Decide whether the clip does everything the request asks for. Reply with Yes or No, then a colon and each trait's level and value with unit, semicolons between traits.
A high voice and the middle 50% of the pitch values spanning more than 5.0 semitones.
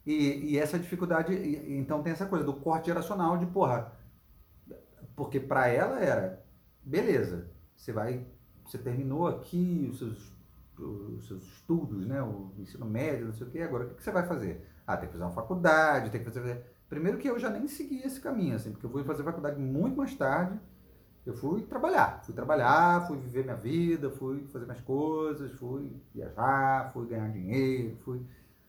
No: low, 135 Hz; wide, 5.5 semitones